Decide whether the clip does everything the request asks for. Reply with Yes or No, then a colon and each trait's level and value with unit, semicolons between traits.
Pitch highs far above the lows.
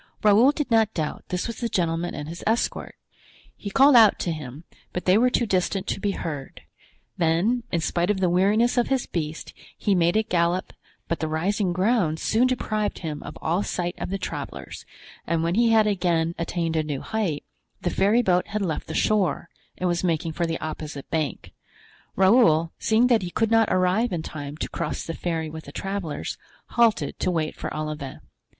No: average, 4.8 semitones